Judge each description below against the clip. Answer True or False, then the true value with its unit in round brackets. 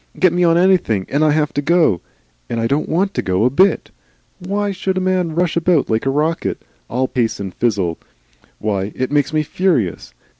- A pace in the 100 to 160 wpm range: False (200 wpm)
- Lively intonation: True (7.7 semitones)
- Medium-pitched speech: True (150 Hz)